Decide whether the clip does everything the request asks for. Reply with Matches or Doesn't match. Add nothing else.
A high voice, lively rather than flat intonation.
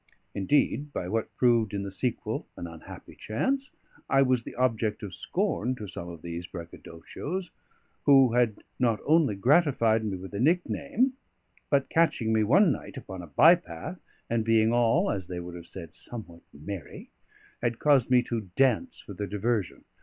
Doesn't match